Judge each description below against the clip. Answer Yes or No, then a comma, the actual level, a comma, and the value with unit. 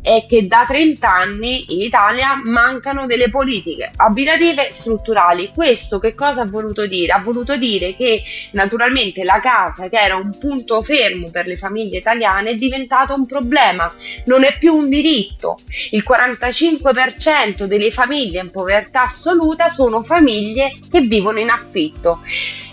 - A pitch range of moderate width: Yes, average, 4.8 semitones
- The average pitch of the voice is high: Yes, high, 240 Hz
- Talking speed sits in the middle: Yes, average, 150 wpm